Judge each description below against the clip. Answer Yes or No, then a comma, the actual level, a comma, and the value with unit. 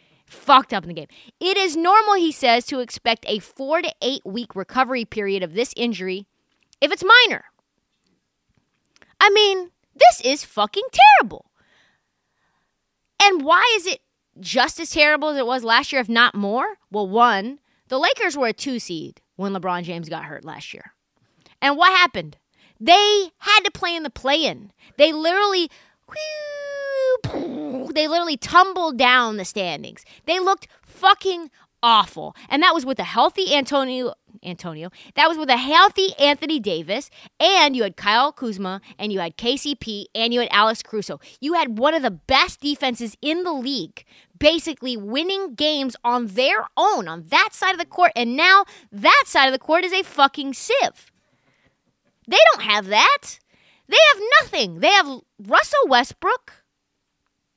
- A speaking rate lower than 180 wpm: Yes, average, 165 wpm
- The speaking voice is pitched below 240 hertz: No, very high, 280 Hz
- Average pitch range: No, wide, 6.6 semitones